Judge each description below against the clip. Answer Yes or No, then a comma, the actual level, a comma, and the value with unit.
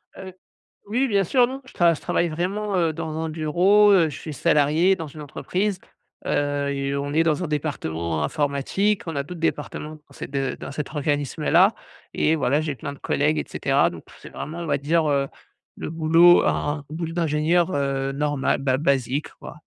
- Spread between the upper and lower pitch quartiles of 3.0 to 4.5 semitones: Yes, average, 3.4 semitones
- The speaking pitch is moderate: Yes, medium, 155 Hz